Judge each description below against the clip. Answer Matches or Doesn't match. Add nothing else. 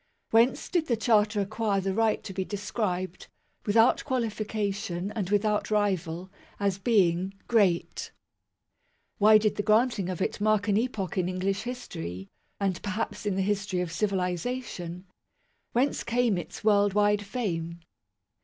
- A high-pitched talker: Matches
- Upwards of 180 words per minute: Doesn't match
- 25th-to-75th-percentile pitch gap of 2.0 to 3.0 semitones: Matches